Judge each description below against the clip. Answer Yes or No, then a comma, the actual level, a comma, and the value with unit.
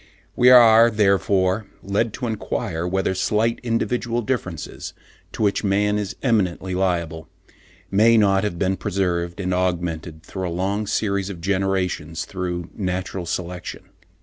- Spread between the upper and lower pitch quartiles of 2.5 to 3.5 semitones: Yes, average, 2.8 semitones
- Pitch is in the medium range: No, very low, 95 Hz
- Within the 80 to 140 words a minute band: Yes, slow, 135 wpm